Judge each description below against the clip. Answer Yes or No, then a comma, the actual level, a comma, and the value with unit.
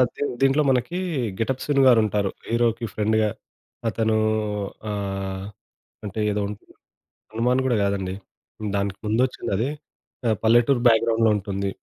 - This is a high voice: No, low, 110 Hz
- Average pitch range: Yes, average, 3.2 semitones